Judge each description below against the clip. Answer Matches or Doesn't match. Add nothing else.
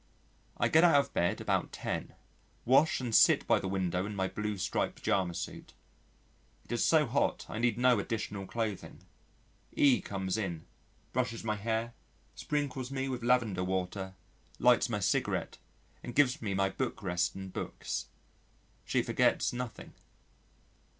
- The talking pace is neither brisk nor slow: Matches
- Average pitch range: Matches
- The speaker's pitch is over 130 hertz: Doesn't match